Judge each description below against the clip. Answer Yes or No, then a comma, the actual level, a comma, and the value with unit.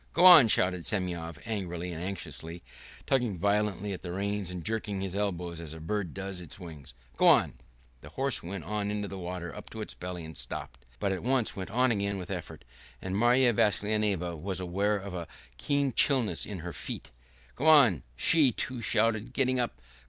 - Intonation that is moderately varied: Yes, average, 4.0 semitones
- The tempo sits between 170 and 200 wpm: Yes, average, 195 wpm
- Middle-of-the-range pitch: No, low, 100 Hz